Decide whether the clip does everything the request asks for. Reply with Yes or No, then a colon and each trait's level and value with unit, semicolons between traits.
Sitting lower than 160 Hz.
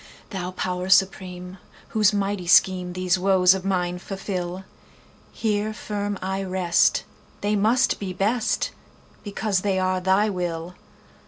No: high, 190 Hz